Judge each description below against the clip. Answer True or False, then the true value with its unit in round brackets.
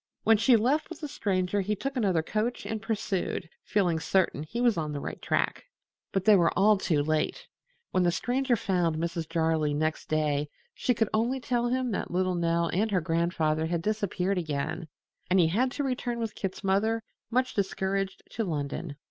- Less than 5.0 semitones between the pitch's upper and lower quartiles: False (5.3 semitones)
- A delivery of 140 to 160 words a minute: False (190 wpm)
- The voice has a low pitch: False (190 Hz)